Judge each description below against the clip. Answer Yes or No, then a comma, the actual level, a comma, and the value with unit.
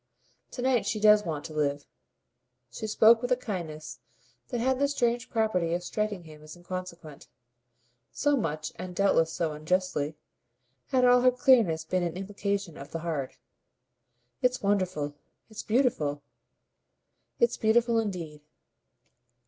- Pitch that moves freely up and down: Yes, wide, 6.5 semitones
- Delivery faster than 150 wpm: No, average, 140 wpm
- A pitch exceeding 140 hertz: Yes, medium, 185 Hz